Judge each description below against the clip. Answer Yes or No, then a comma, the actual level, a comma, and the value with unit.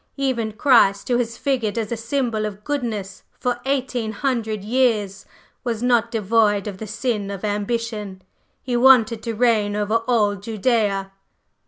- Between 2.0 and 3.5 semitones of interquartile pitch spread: Yes, average, 2.8 semitones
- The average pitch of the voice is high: Yes, high, 225 Hz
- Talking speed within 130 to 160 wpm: Yes, average, 150 wpm